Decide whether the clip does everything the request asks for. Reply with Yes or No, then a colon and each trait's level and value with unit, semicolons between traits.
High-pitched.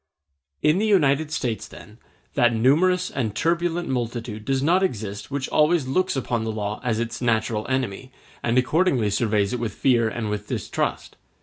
No: low, 125 Hz